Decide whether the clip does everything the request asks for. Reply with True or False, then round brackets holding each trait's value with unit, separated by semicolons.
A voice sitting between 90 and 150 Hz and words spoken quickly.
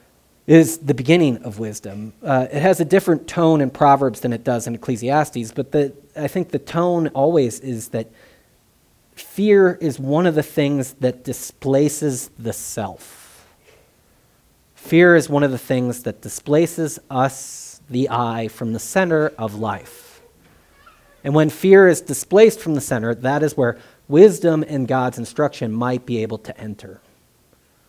False (135 Hz; 155 wpm)